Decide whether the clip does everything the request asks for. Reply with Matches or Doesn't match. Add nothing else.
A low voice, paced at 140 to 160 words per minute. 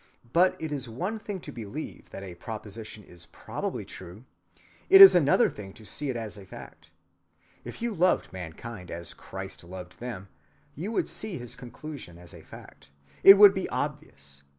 Doesn't match